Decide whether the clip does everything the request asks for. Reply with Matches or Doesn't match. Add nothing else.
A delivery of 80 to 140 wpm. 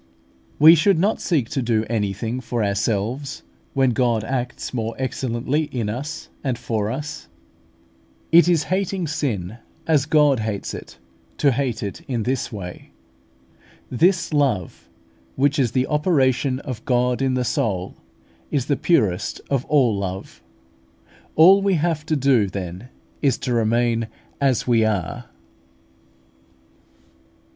Matches